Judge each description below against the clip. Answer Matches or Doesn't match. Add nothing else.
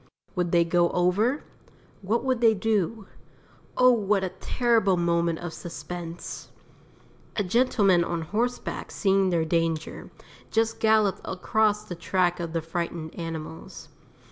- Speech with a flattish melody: Doesn't match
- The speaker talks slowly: Matches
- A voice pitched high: Doesn't match